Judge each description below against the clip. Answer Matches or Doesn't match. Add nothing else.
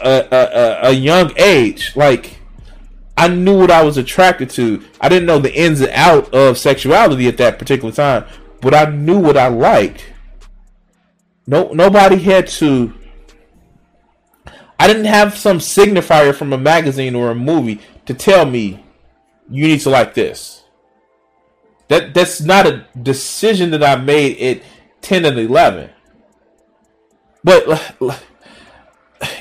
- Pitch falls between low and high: Matches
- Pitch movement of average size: Doesn't match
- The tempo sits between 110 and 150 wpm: Matches